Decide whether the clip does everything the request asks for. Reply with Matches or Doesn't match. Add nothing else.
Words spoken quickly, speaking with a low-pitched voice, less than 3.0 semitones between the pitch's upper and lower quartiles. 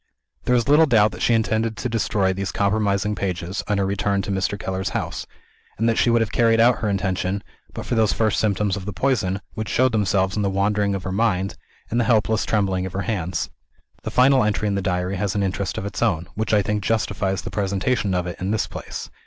Matches